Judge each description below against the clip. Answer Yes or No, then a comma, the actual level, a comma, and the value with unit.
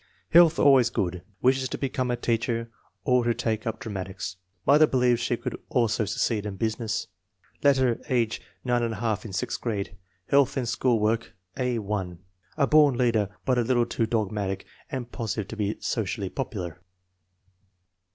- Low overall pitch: Yes, low, 115 Hz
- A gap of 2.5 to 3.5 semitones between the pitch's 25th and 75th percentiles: Yes, average, 3.0 semitones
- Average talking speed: Yes, average, 155 wpm